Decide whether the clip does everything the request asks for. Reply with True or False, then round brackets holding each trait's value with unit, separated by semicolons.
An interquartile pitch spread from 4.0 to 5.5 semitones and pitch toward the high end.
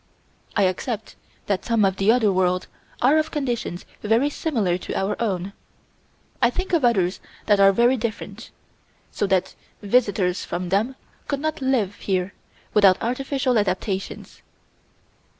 True (4.7 semitones; 210 Hz)